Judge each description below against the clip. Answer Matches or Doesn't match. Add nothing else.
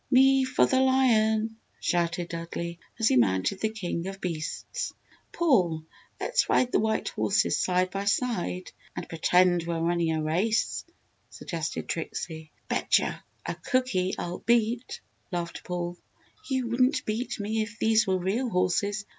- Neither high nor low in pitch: Doesn't match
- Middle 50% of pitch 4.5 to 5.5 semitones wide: Matches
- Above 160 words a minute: Doesn't match